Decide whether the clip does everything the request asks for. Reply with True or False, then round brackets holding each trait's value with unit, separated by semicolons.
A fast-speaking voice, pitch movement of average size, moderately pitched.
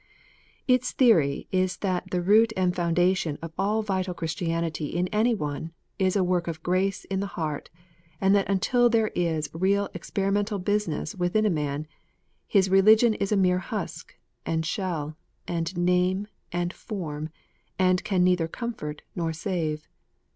False (155 wpm; 3.3 semitones; 180 Hz)